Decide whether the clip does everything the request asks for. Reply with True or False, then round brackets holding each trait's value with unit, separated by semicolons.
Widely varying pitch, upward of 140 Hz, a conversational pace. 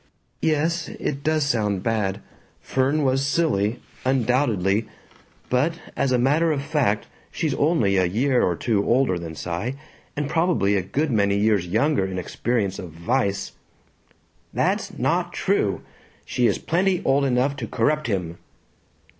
False (6.6 semitones; 125 Hz; 145 wpm)